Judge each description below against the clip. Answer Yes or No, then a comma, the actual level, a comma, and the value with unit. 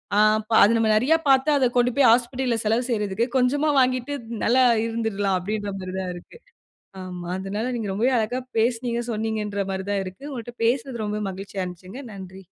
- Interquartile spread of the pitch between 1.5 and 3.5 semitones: No, average, 4.1 semitones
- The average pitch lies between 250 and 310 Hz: No, high, 220 Hz